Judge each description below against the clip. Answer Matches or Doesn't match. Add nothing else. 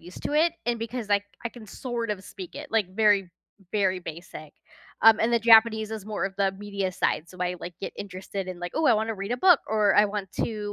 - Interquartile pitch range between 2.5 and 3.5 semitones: Matches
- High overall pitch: Matches